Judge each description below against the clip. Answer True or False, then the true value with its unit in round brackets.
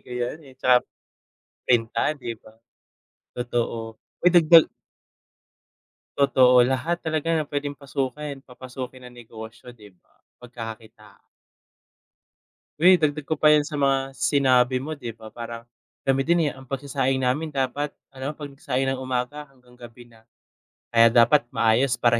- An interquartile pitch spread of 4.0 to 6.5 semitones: False (3.2 semitones)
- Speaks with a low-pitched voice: True (130 Hz)